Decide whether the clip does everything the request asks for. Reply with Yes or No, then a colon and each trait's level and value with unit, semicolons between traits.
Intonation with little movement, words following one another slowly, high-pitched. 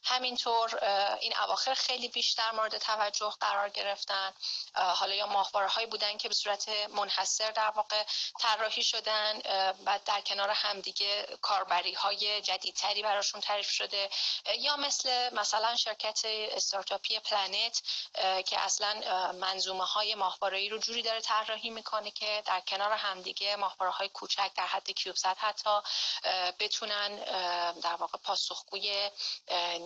No: narrow, 2.0 semitones; average, 125 wpm; high, 205 Hz